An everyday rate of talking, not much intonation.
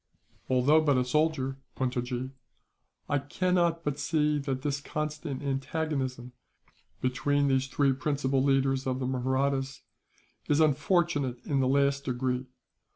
No: slow, 125 wpm; narrow, 2.1 semitones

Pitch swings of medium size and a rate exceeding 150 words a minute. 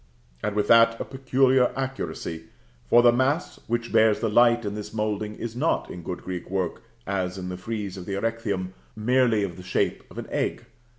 Yes: average, 3.8 semitones; average, 195 wpm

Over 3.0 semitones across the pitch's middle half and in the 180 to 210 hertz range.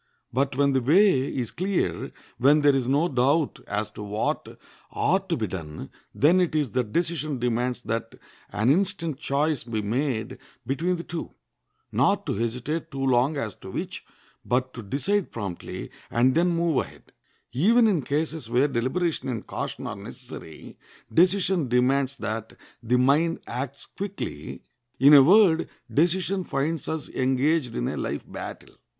No: average, 5.3 semitones; medium, 140 Hz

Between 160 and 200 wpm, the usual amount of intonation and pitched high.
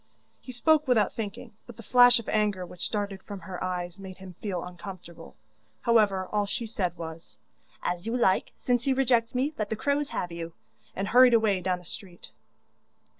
Yes: average, 185 wpm; average, 4.6 semitones; high, 205 Hz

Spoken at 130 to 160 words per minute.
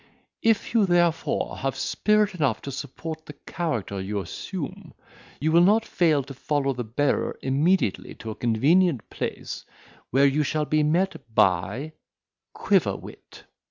Yes: average, 140 wpm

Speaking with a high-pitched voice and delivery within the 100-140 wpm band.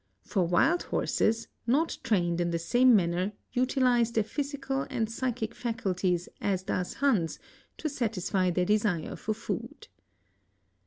Yes: high, 220 Hz; slow, 135 wpm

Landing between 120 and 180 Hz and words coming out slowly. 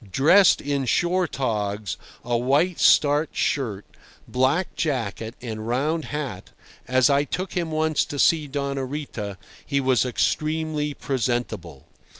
Yes: medium, 140 Hz; slow, 130 wpm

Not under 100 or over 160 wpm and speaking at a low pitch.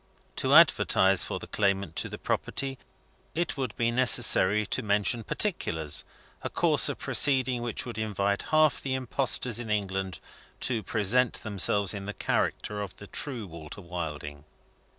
Yes: average, 150 wpm; low, 105 Hz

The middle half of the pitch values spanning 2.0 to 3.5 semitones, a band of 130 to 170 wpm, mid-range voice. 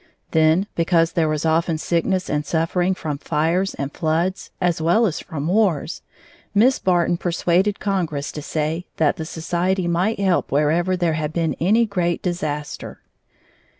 Yes: average, 2.7 semitones; average, 150 wpm; medium, 170 Hz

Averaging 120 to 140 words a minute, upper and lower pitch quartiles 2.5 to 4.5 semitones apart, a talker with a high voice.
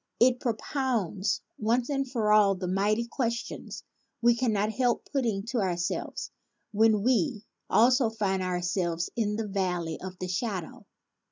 Yes: slow, 135 wpm; average, 3.9 semitones; high, 215 Hz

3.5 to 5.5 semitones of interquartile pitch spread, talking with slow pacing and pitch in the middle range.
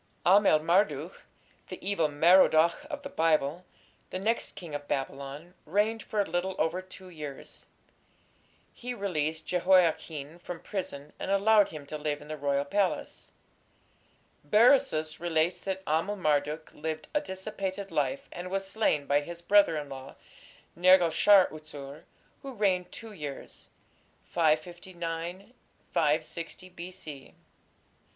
Yes: average, 4.0 semitones; slow, 130 wpm; medium, 170 Hz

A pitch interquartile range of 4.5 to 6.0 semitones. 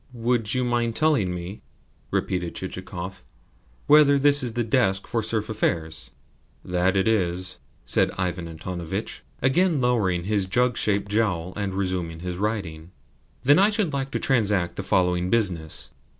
Yes: average, 5.2 semitones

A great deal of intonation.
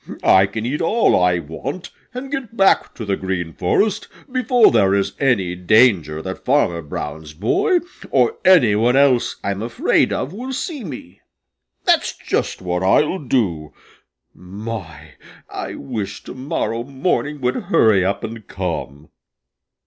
Yes: wide, 8.2 semitones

